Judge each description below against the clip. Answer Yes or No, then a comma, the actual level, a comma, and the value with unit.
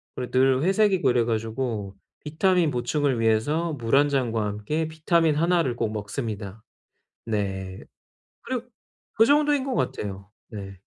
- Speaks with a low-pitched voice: Yes, low, 130 Hz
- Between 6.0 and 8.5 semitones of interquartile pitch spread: Yes, wide, 7.0 semitones